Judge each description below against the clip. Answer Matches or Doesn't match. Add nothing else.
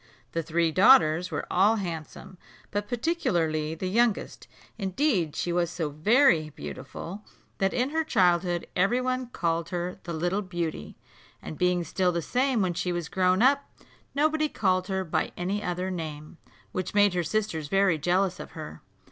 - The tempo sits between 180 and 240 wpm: Doesn't match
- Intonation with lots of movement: Doesn't match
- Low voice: Doesn't match